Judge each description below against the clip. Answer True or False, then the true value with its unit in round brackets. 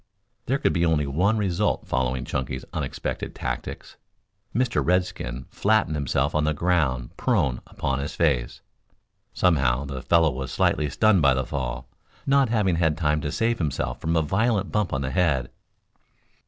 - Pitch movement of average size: False (5.7 semitones)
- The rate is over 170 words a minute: False (160 wpm)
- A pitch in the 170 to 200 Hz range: False (75 Hz)